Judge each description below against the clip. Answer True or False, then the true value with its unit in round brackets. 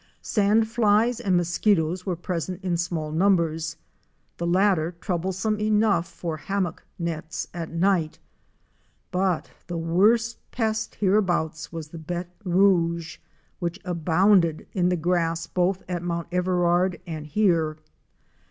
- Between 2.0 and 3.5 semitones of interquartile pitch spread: True (2.8 semitones)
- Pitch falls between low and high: True (175 Hz)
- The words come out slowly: True (125 wpm)